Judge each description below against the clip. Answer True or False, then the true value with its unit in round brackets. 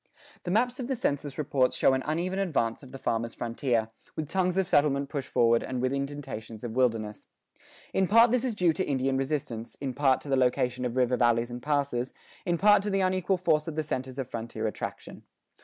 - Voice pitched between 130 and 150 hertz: True (140 Hz)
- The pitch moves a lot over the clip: True (6.1 semitones)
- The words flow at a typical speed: False (210 wpm)